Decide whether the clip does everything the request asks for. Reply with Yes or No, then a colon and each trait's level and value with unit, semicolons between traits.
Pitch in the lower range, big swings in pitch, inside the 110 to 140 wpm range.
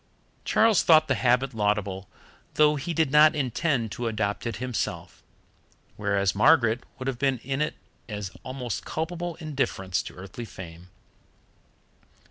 Yes: low, 125 Hz; wide, 6.5 semitones; slow, 135 wpm